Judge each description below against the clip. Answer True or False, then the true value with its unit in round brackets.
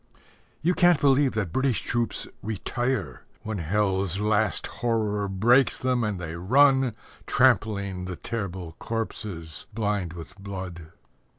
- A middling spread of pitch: True (4.6 semitones)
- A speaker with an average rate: False (120 wpm)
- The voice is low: True (105 Hz)